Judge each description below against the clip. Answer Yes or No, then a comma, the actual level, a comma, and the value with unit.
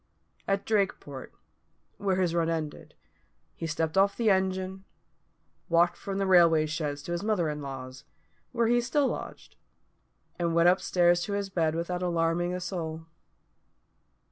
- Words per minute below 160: Yes, average, 150 wpm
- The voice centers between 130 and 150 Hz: No, medium, 175 Hz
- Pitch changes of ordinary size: Yes, average, 3.0 semitones